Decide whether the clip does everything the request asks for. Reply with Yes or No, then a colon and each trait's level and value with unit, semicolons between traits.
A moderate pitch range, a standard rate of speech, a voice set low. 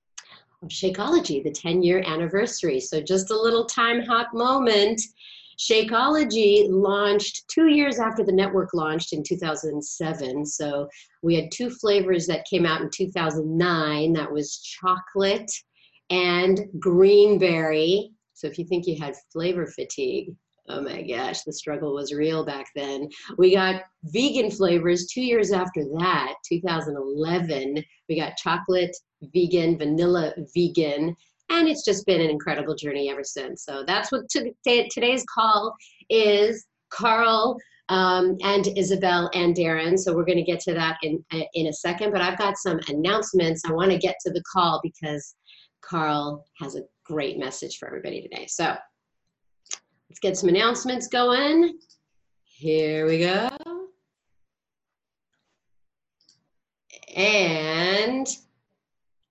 No: average, 4.8 semitones; average, 145 wpm; medium, 180 Hz